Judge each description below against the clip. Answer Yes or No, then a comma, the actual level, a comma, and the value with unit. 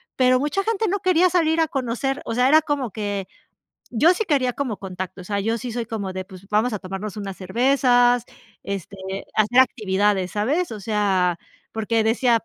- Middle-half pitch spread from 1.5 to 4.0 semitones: No, average, 5.2 semitones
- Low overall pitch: No, high, 230 Hz